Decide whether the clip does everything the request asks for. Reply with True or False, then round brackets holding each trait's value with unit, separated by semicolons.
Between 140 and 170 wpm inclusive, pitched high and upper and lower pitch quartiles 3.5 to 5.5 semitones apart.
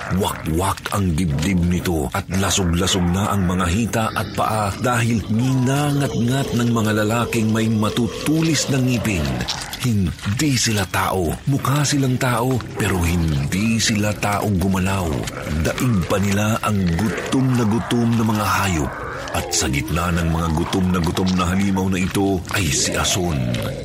False (145 wpm; 105 Hz; 4.0 semitones)